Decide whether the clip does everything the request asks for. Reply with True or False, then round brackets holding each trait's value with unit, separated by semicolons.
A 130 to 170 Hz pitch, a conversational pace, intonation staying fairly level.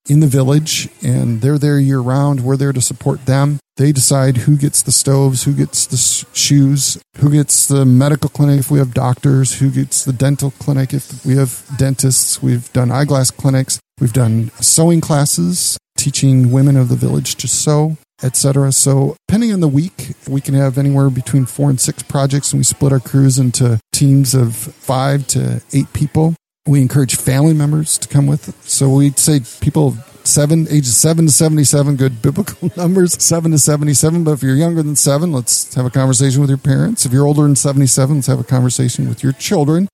True (140 Hz; 195 wpm; 1.9 semitones)